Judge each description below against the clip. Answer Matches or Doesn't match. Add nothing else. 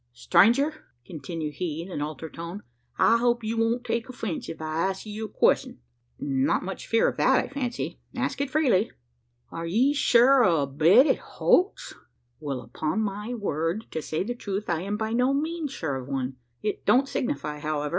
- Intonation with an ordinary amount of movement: Doesn't match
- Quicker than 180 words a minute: Matches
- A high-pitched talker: Matches